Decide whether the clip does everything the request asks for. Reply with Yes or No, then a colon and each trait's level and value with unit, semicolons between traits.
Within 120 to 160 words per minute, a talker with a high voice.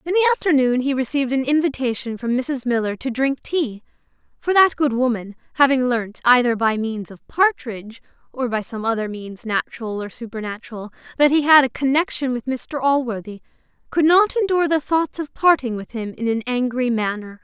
No: average, 180 wpm; very high, 255 Hz